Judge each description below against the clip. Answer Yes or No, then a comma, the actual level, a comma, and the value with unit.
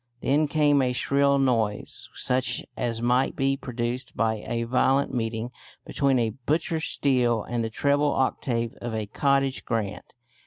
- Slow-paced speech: No, average, 150 wpm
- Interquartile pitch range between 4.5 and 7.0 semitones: No, average, 2.9 semitones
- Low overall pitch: Yes, low, 125 Hz